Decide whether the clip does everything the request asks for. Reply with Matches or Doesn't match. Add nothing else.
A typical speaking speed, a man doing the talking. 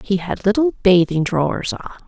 Doesn't match